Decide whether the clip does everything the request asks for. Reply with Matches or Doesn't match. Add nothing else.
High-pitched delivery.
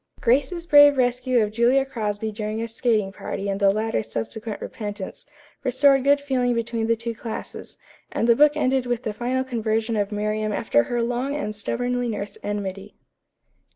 Matches